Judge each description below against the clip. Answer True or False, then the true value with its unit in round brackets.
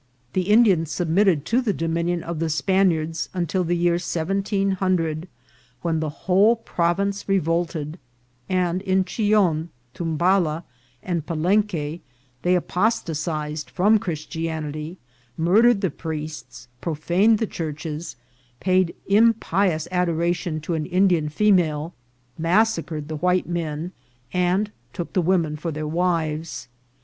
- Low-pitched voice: False (175 Hz)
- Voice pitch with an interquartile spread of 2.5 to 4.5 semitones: True (3.0 semitones)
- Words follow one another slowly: True (120 wpm)